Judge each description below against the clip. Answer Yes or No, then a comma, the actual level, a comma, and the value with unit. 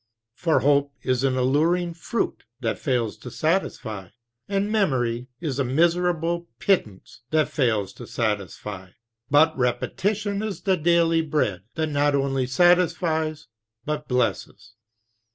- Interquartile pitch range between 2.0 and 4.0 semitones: No, wide, 5.5 semitones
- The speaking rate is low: Yes, slow, 125 wpm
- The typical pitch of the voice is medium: Yes, medium, 150 Hz